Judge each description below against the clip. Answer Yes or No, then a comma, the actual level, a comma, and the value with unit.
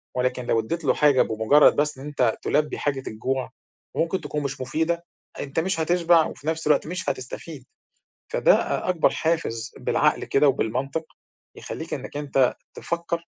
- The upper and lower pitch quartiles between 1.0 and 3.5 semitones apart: No, average, 4.0 semitones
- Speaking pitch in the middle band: Yes, medium, 145 Hz